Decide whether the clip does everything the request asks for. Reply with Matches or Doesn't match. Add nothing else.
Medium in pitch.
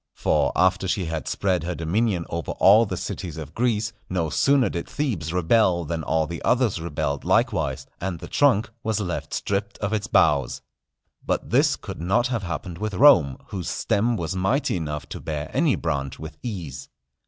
Doesn't match